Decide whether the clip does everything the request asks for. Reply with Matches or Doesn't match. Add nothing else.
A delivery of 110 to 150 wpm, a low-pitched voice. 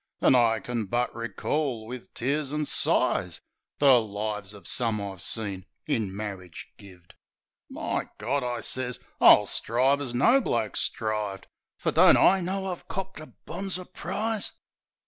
Matches